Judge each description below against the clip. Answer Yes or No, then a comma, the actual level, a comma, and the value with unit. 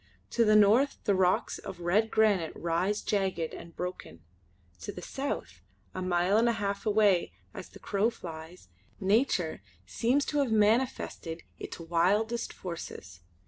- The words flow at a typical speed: Yes, average, 145 wpm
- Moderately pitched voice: No, high, 195 Hz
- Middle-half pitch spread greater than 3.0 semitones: Yes, average, 4.3 semitones